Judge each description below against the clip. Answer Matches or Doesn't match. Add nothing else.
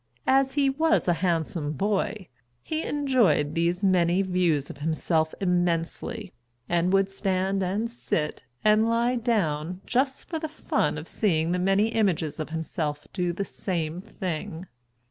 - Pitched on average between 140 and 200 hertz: Matches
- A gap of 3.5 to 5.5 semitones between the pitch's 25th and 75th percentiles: Matches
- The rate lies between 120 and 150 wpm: Matches